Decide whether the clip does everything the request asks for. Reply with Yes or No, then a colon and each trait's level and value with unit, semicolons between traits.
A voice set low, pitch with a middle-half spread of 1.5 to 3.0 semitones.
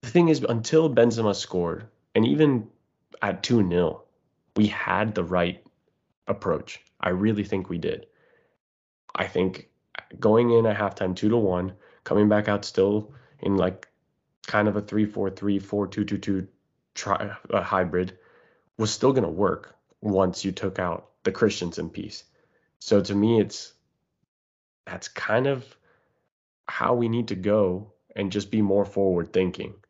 Yes: low, 100 Hz; average, 2.7 semitones